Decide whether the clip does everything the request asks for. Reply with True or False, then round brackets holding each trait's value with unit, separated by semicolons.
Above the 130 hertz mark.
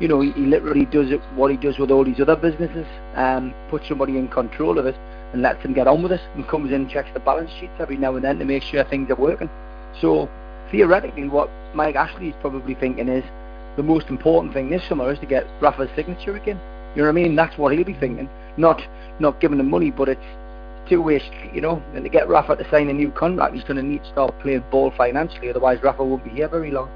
True (140 Hz)